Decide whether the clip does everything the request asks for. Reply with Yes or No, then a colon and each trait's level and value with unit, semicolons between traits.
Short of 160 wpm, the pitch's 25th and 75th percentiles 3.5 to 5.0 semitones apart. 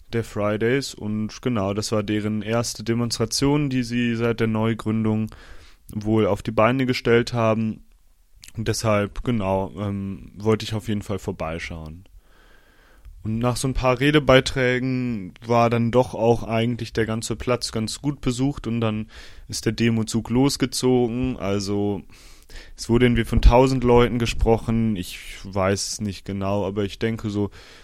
No: average, 150 wpm; average, 2.9 semitones